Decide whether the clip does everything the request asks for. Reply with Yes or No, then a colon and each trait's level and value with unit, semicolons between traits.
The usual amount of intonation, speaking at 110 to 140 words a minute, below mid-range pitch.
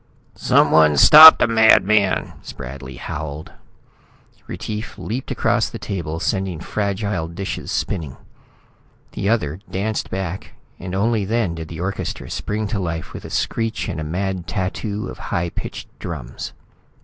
Yes: average, 4.7 semitones; slow, 135 wpm; very low, 95 Hz